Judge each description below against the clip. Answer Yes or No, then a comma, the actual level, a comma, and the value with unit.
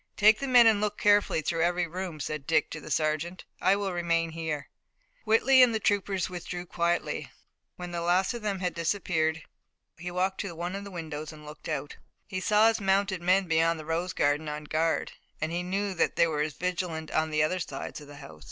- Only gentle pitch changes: No, average, 3.4 semitones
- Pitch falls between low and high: Yes, medium, 175 Hz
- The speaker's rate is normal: No, fast, 215 wpm